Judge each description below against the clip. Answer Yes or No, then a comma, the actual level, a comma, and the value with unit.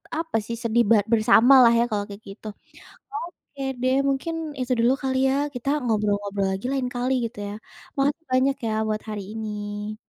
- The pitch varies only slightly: No, average, 4.0 semitones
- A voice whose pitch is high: Yes, high, 235 Hz